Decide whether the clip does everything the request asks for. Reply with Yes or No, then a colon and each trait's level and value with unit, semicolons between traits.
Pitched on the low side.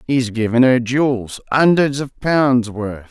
Yes: low, 125 Hz